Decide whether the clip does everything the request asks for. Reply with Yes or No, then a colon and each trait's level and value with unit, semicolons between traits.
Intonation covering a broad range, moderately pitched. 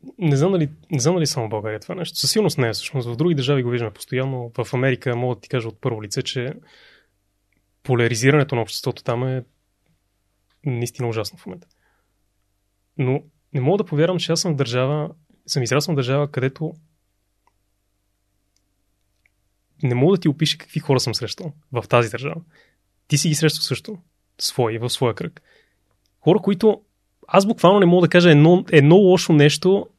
No: wide, 6.5 semitones; low, 130 Hz